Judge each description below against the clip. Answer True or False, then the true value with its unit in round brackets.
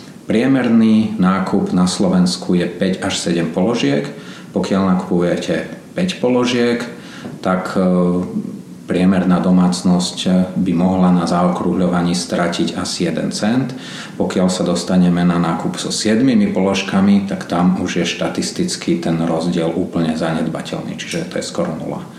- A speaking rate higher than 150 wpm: False (125 wpm)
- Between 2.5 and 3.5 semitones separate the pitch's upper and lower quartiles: True (2.8 semitones)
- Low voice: True (90 Hz)